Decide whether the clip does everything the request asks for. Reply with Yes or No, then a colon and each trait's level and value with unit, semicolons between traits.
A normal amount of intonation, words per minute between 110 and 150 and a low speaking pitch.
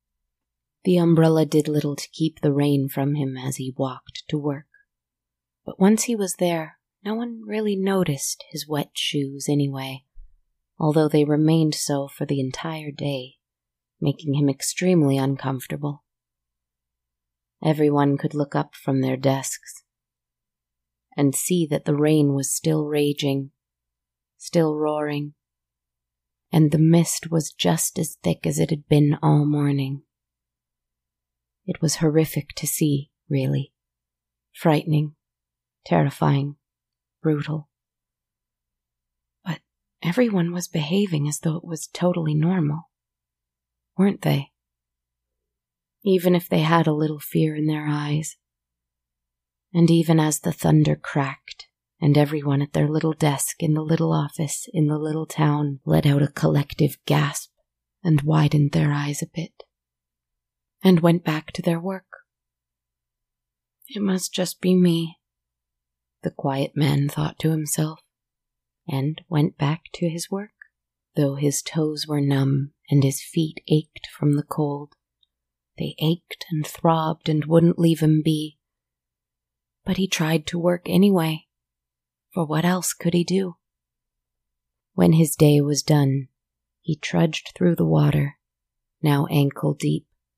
No: average, 4.4 semitones; slow, 135 wpm; medium, 145 Hz